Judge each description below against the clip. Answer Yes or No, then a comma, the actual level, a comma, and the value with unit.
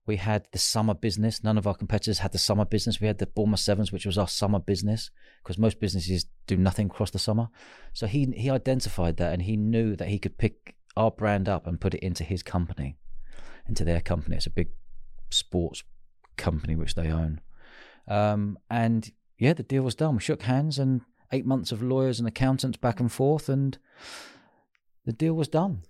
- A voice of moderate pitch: No, low, 105 Hz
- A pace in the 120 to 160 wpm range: No, fast, 205 wpm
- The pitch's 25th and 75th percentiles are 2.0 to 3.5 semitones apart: No, average, 4.0 semitones